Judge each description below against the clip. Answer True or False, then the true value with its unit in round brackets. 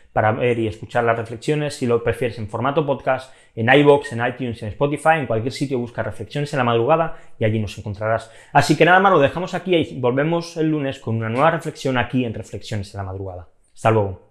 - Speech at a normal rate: False (220 wpm)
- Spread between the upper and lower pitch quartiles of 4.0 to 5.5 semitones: True (4.6 semitones)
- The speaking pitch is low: True (125 Hz)